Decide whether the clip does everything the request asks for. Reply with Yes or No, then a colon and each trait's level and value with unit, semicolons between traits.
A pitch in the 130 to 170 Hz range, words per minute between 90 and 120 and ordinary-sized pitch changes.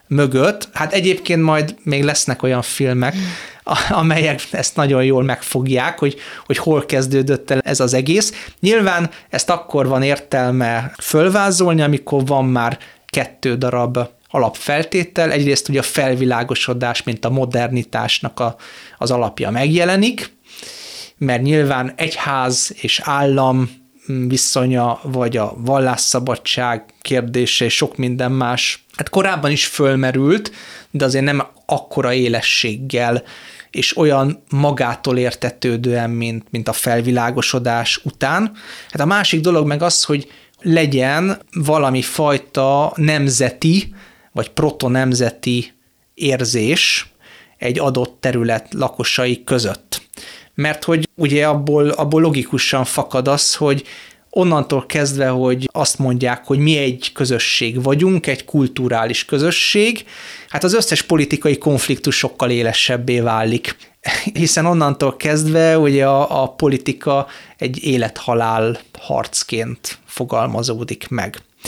Yes: low, 135 Hz; average, 115 wpm; average, 3.3 semitones